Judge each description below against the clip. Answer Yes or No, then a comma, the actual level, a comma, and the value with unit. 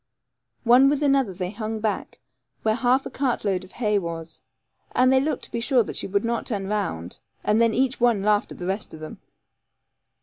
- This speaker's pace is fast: Yes, fast, 210 wpm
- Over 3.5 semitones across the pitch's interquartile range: Yes, average, 4.4 semitones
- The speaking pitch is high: Yes, high, 220 Hz